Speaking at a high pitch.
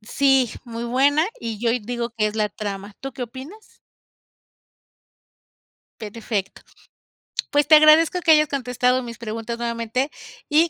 Yes: high, 240 Hz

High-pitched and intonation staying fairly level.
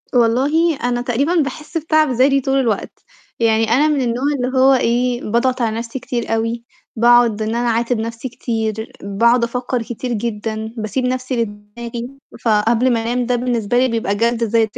Yes: high, 235 Hz; narrow, 2.1 semitones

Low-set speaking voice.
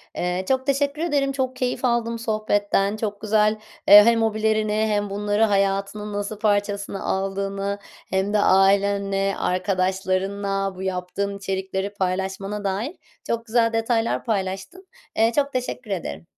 No: high, 205 Hz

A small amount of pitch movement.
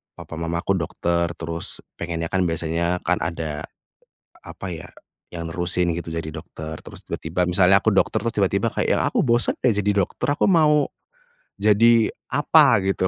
No: average, 3.5 semitones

